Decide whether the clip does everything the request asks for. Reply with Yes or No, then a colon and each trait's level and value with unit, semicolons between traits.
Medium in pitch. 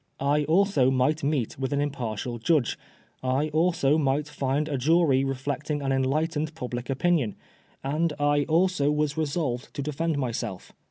Yes: medium, 145 Hz